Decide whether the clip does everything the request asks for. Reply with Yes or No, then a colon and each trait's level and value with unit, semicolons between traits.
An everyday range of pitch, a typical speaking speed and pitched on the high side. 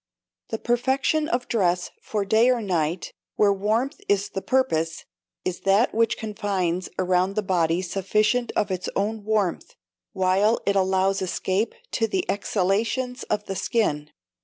Yes: average, 3.3 semitones; average, 145 wpm; high, 200 Hz